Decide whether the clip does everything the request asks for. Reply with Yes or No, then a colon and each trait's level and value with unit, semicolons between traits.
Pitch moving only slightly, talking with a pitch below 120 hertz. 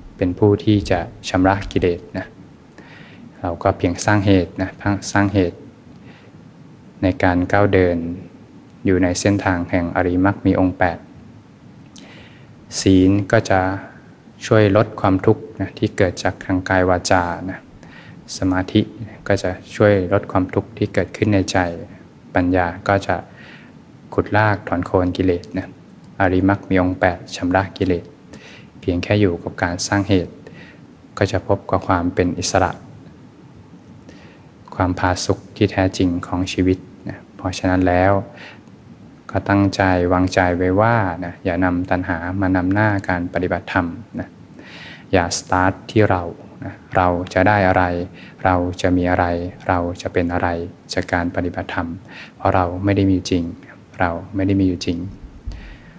Yes: narrow, 1.7 semitones; very low, 95 Hz